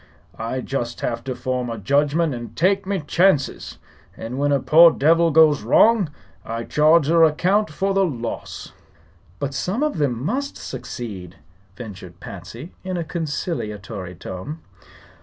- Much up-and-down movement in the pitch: Yes, wide, 6.3 semitones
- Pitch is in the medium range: Yes, medium, 145 Hz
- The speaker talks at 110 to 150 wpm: Yes, average, 145 wpm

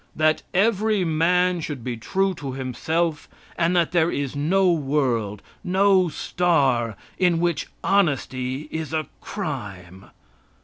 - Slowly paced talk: Yes, slow, 125 wpm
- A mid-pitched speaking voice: Yes, medium, 160 Hz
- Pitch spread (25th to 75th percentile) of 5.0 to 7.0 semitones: Yes, wide, 5.4 semitones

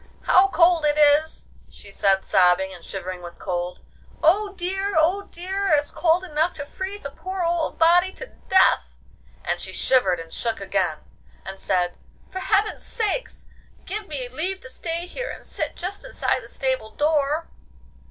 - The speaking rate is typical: Yes, average, 165 wpm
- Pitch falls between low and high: No, very high, 315 Hz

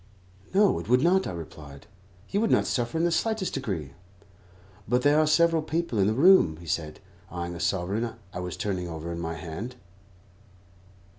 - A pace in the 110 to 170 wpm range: No, average, 180 wpm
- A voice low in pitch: Yes, low, 105 Hz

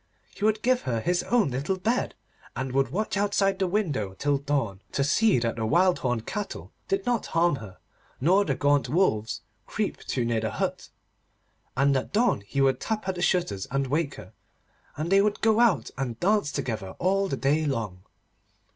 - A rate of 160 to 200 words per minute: Yes, average, 190 wpm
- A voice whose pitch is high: No, medium, 145 Hz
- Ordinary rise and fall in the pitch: No, wide, 7.7 semitones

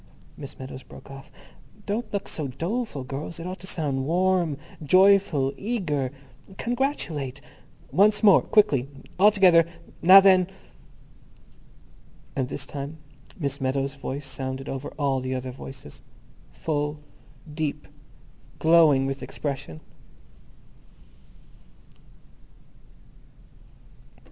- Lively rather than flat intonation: Yes, wide, 5.7 semitones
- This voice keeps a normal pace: No, slow, 100 wpm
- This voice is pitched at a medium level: Yes, medium, 150 Hz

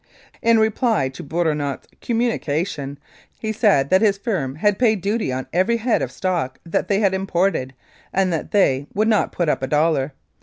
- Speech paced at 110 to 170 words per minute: No, average, 180 wpm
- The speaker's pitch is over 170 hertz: Yes, medium, 185 Hz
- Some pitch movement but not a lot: No, wide, 6.8 semitones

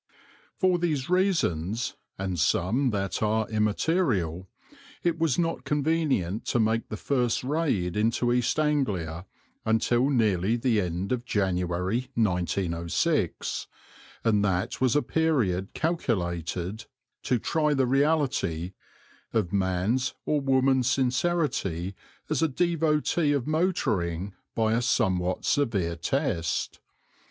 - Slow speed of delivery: Yes, slow, 115 wpm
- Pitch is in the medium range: No, low, 115 Hz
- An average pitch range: No, wide, 7.5 semitones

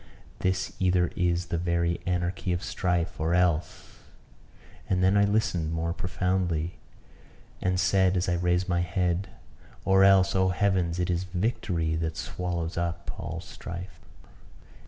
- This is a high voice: No, very low, 90 Hz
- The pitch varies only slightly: Yes, narrow, 1.6 semitones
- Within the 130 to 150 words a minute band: Yes, average, 140 wpm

